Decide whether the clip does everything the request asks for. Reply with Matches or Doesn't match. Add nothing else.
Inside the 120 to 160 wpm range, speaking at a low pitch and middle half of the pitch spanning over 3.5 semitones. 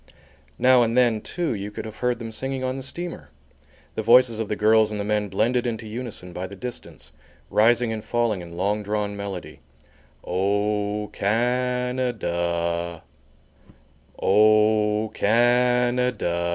Doesn't match